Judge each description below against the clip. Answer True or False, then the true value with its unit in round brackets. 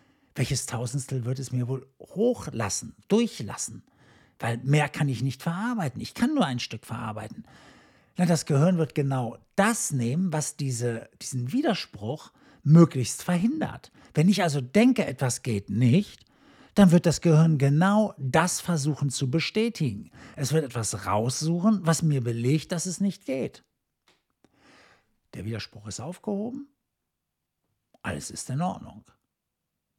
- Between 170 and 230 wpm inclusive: False (135 wpm)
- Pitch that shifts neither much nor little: False (6.4 semitones)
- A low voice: False (150 Hz)